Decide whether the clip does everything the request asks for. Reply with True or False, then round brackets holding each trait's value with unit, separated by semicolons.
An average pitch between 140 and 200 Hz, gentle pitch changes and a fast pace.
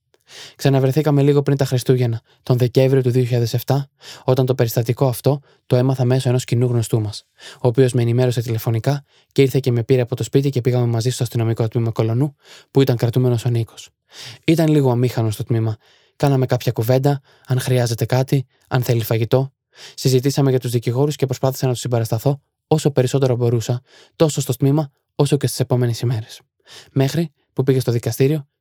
False (130 Hz; 2.0 semitones; 175 wpm)